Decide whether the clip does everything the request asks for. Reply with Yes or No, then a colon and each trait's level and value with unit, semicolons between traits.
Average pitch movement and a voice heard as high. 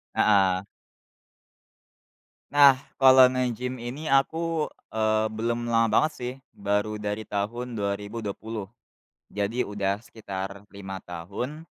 No: average, 3.9 semitones; low, 110 Hz